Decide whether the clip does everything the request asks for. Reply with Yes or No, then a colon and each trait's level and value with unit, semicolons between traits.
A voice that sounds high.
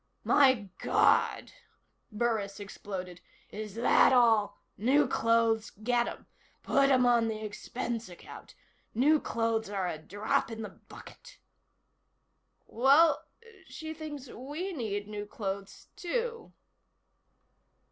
Yes: high, 230 Hz